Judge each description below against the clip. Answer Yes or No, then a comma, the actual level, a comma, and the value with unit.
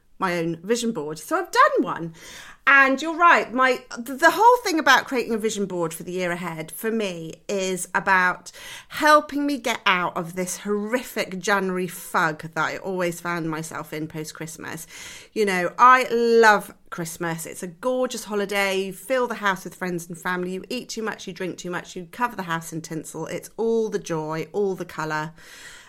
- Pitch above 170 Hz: Yes, high, 190 Hz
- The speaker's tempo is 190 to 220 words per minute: Yes, average, 200 wpm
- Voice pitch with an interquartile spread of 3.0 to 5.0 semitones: No, wide, 5.5 semitones